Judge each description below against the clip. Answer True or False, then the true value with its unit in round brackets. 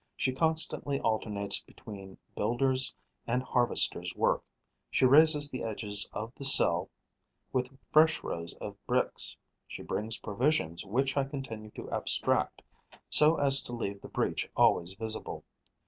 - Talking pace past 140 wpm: False (135 wpm)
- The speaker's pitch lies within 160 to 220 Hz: False (125 Hz)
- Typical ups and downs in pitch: True (4.7 semitones)